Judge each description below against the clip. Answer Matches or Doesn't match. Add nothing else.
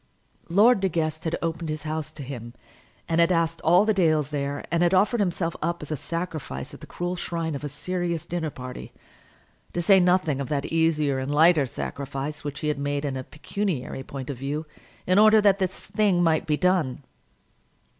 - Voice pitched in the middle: Matches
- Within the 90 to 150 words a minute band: Doesn't match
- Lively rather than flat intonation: Doesn't match